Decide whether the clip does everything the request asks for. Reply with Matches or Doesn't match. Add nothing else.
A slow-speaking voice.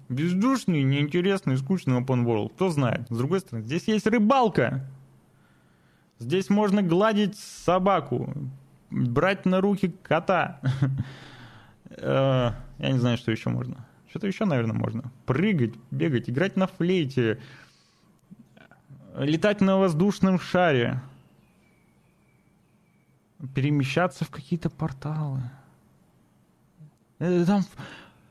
Matches